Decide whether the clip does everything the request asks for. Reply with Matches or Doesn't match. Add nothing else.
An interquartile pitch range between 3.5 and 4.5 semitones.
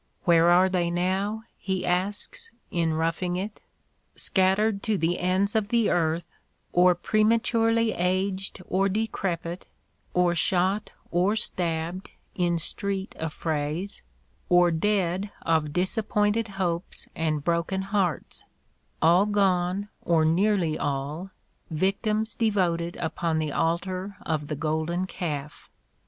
Doesn't match